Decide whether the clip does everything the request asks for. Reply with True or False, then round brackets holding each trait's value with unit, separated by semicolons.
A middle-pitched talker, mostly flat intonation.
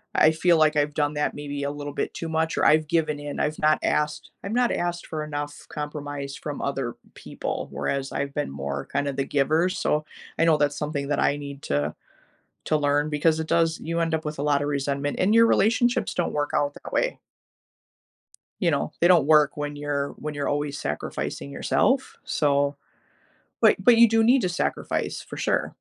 True (150 Hz; 2.0 semitones)